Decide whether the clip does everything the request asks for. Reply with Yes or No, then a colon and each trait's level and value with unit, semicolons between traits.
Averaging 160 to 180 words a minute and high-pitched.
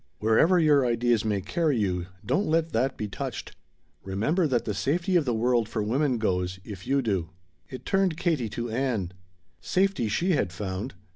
No: average, 175 wpm; low, 120 Hz